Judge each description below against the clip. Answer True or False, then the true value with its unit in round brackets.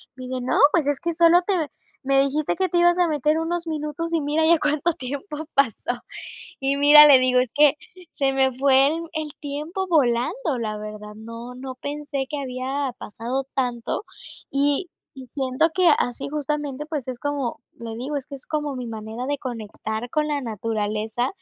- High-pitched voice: True (275 Hz)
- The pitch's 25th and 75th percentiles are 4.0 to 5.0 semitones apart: False (3.4 semitones)